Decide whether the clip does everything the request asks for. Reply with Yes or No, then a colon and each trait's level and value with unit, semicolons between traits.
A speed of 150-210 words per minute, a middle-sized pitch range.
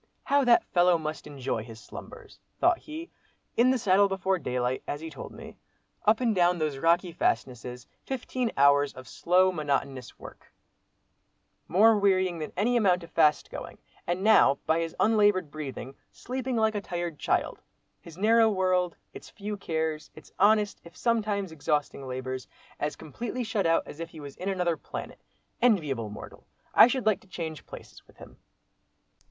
No: average, 160 wpm; wide, 6.0 semitones